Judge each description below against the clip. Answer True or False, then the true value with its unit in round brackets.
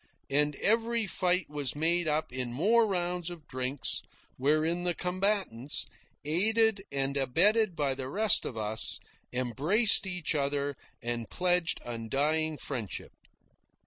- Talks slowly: True (125 wpm)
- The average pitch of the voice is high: False (155 Hz)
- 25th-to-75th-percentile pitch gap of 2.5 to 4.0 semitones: False (5.2 semitones)